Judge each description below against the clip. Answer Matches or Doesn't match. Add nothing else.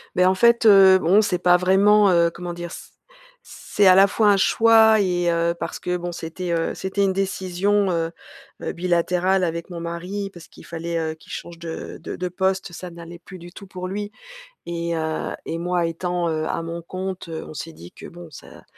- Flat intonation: Matches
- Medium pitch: Matches